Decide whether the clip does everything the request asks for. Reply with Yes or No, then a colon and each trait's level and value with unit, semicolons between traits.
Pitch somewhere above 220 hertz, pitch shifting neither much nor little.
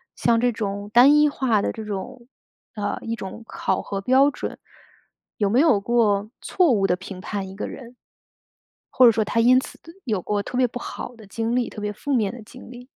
Yes: high, 230 Hz; average, 3.5 semitones